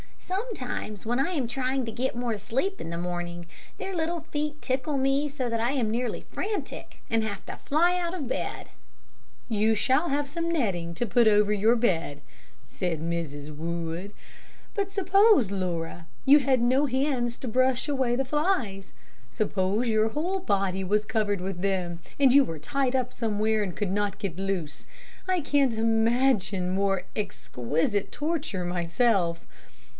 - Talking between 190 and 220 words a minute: No, average, 160 wpm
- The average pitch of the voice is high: Yes, high, 225 Hz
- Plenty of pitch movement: Yes, wide, 6.1 semitones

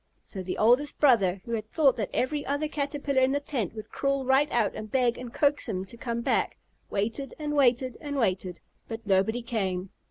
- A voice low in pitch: No, high, 240 Hz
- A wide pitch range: No, average, 4.7 semitones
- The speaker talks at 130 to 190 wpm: No, average, 200 wpm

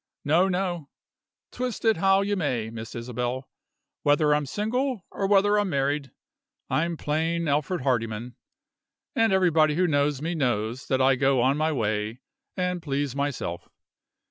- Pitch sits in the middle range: Yes, medium, 150 Hz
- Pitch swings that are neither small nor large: No, wide, 5.7 semitones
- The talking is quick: No, average, 145 wpm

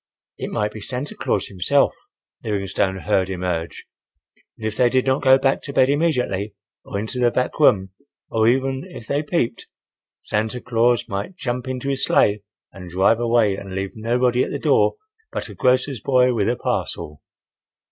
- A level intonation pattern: No, average, 4.6 semitones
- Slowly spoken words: No, average, 175 wpm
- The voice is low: Yes, low, 120 Hz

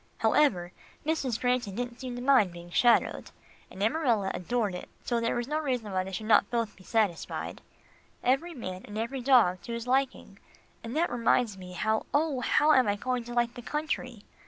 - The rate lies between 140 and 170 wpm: No, average, 200 wpm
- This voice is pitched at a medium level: No, high, 235 Hz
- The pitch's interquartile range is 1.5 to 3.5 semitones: No, average, 4.0 semitones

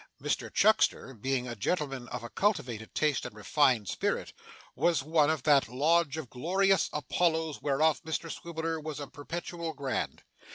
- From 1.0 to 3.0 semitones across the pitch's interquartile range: No, average, 3.8 semitones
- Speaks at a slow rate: No, average, 150 wpm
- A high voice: No, medium, 150 Hz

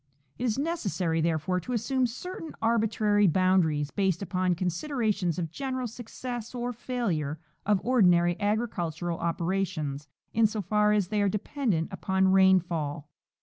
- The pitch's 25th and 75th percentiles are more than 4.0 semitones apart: Yes, average, 5.1 semitones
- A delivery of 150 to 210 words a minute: No, average, 140 wpm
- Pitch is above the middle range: Yes, high, 195 Hz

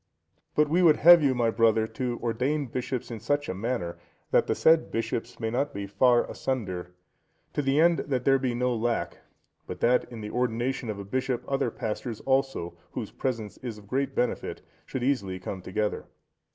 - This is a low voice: Yes, low, 120 Hz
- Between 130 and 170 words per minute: No, average, 190 wpm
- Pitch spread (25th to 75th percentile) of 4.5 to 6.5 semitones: No, average, 3.4 semitones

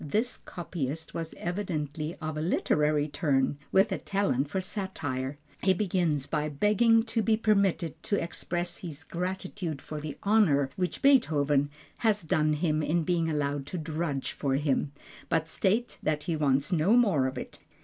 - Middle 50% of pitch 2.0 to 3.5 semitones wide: No, average, 4.5 semitones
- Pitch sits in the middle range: Yes, medium, 160 Hz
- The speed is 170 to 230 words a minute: No, average, 160 wpm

